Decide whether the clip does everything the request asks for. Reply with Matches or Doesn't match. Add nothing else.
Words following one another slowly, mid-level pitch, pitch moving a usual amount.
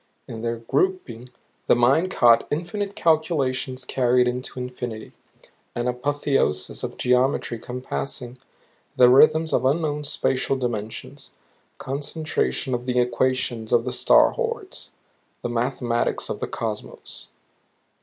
Doesn't match